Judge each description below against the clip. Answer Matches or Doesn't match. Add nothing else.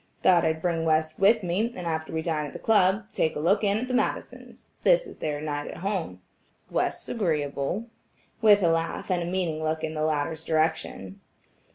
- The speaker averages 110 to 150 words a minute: Doesn't match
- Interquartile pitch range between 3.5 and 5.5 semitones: Matches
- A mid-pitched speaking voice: Matches